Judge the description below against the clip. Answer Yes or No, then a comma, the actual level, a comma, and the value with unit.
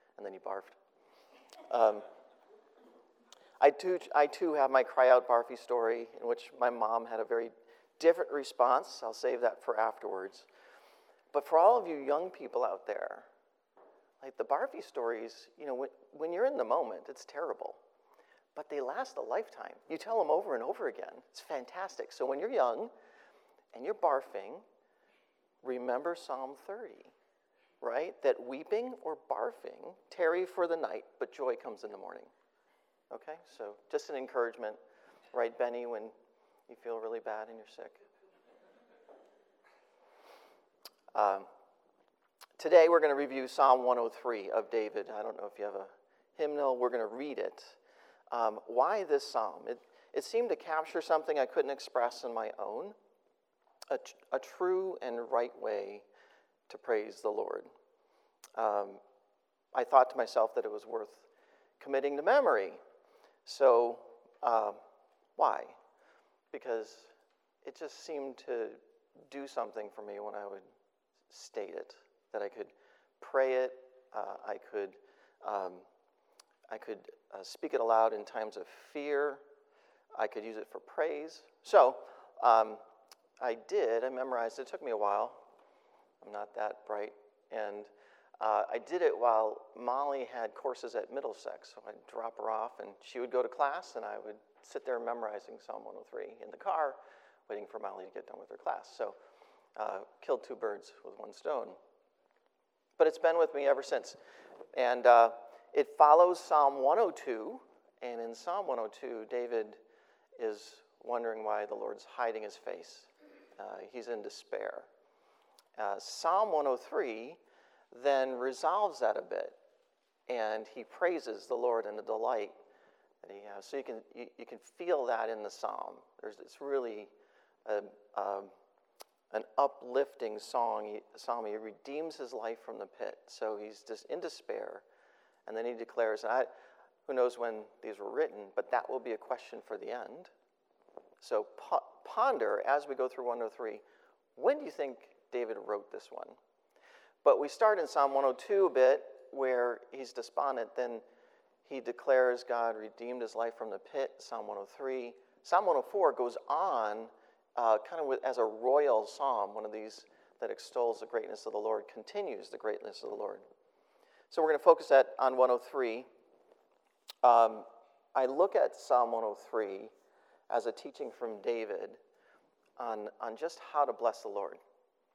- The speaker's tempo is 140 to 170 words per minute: Yes, average, 160 wpm